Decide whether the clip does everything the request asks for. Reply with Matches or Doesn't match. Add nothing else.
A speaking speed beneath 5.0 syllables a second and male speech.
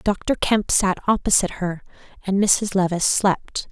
Doesn't match